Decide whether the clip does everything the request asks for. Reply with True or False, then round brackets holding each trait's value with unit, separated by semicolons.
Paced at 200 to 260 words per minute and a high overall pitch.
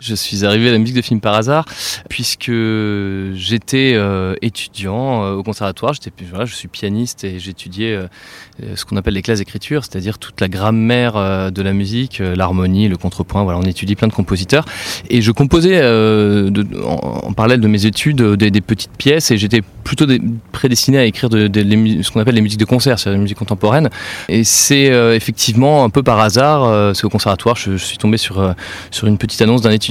False (220 wpm; 110 Hz)